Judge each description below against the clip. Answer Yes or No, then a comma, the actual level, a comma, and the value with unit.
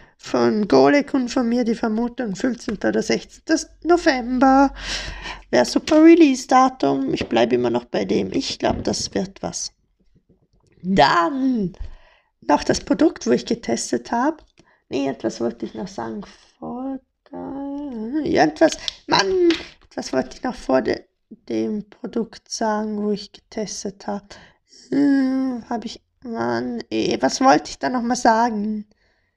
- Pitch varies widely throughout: Yes, wide, 6.3 semitones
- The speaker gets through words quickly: No, average, 140 wpm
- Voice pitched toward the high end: Yes, high, 240 Hz